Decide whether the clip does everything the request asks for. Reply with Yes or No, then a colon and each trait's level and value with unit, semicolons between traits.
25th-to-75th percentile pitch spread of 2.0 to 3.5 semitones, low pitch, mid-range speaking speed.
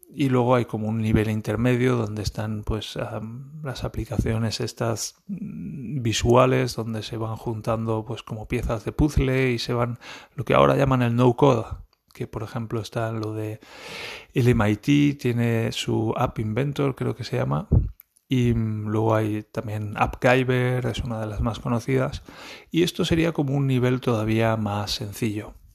Yes: average, 2.7 semitones; low, 115 Hz; average, 165 wpm